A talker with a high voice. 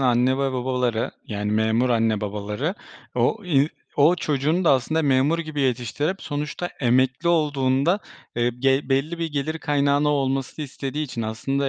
No: low, 135 Hz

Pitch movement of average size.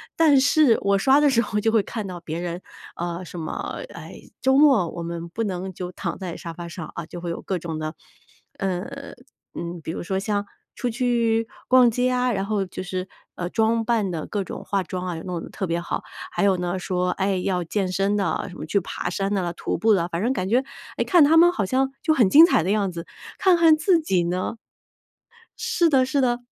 No: wide, 5.8 semitones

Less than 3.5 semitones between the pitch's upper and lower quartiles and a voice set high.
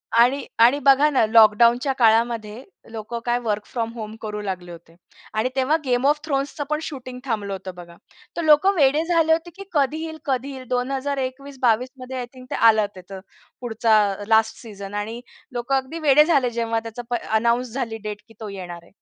No: average, 4.0 semitones; high, 240 Hz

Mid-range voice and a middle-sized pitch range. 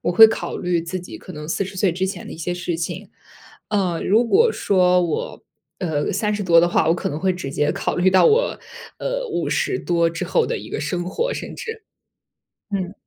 Yes: medium, 180 Hz; average, 3.6 semitones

